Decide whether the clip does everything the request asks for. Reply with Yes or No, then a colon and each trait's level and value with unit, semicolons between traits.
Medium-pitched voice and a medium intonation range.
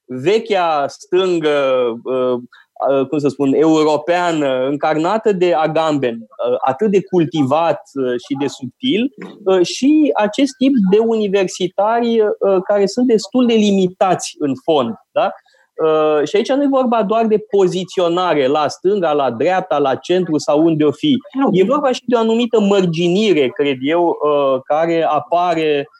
No: medium, 180 Hz; wide, 6.5 semitones